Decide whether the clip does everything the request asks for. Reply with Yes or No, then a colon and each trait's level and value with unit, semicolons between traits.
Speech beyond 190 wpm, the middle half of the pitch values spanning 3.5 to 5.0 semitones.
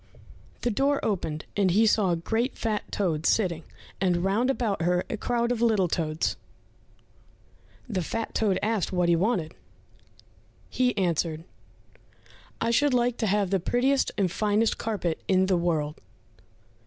No: average, 150 wpm; average, 4.7 semitones